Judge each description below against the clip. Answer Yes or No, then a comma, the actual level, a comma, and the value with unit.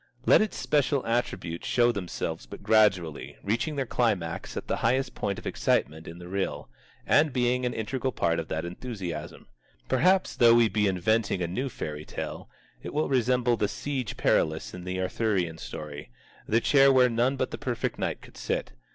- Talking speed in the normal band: Yes, average, 180 wpm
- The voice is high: No, low, 110 Hz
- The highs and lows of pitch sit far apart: Yes, wide, 6.3 semitones